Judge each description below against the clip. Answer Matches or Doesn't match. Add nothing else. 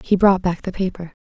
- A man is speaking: Doesn't match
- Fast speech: Matches